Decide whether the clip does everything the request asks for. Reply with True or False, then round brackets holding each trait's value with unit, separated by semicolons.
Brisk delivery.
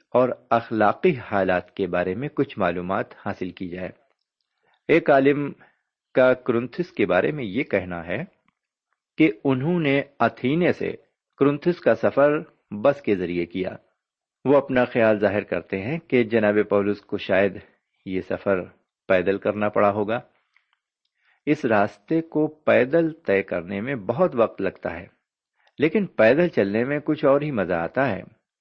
False (150 wpm)